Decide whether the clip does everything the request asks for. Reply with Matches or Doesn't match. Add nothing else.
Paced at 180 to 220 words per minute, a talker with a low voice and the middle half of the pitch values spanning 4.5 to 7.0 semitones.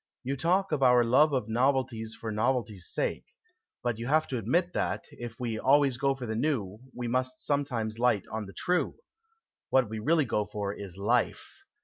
Doesn't match